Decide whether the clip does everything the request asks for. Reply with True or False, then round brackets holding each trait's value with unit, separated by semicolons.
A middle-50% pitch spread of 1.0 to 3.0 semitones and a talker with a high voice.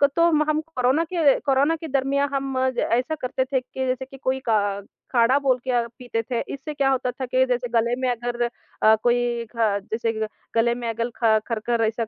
True (2.5 semitones; 250 Hz)